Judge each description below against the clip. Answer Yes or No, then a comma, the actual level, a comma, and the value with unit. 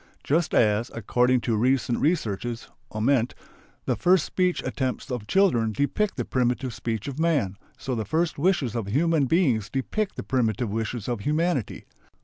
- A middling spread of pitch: No, wide, 5.9 semitones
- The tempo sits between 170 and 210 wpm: No, average, 155 wpm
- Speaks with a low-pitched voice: Yes, low, 125 Hz